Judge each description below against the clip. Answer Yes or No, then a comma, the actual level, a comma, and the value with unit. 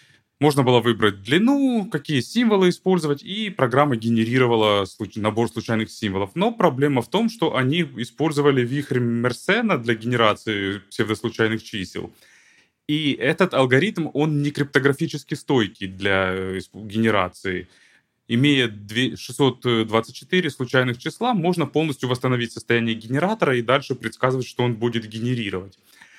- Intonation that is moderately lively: Yes, average, 4.7 semitones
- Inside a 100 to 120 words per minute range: Yes, average, 115 wpm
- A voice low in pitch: Yes, low, 125 Hz